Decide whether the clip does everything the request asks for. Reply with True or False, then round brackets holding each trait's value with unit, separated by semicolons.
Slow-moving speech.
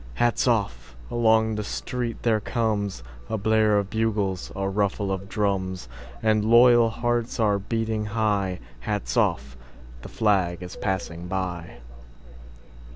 True (105 wpm)